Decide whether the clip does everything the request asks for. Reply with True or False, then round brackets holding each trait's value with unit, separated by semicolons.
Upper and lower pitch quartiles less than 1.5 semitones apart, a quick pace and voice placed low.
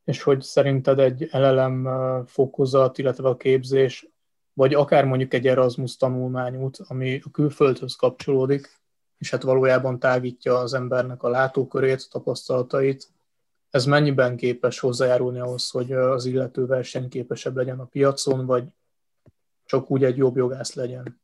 False (1.0 semitones; 135 wpm; 130 Hz)